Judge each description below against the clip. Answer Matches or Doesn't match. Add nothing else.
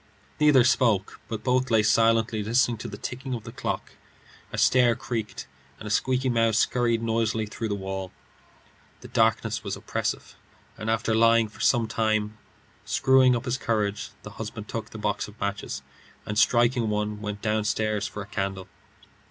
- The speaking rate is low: Doesn't match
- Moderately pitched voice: Doesn't match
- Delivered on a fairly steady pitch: Matches